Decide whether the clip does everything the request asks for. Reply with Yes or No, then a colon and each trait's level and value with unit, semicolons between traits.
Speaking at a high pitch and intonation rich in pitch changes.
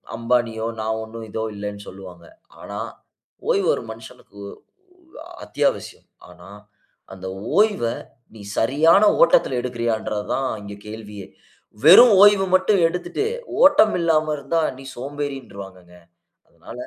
No: low, 120 Hz; wide, 8.1 semitones